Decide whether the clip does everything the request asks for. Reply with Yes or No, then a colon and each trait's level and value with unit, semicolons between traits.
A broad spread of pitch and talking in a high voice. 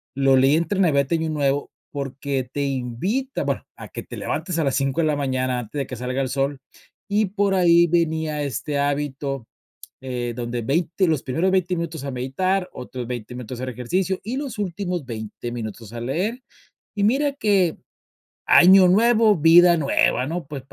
No: wide, 5.9 semitones; medium, 145 Hz